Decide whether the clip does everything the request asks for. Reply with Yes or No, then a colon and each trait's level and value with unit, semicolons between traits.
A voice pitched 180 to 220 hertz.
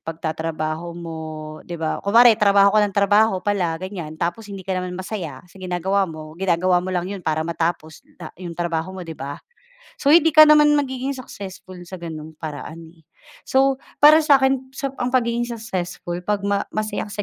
Yes: medium, 185 Hz